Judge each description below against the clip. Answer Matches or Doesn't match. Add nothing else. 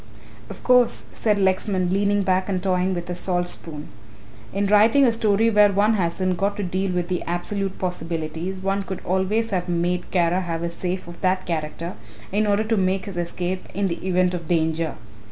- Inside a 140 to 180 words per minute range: Doesn't match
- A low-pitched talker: Doesn't match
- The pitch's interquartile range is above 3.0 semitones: Doesn't match